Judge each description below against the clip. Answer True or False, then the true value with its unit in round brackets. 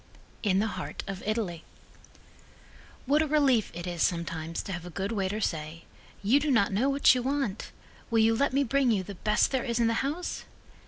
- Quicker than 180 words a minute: True (205 wpm)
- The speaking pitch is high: True (220 Hz)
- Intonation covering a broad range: True (6.1 semitones)